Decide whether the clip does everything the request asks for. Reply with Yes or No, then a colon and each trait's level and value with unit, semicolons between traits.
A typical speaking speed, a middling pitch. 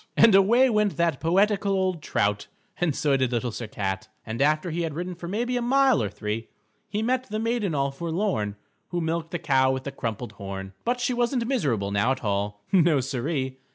No: fast, 210 wpm; medium, 160 Hz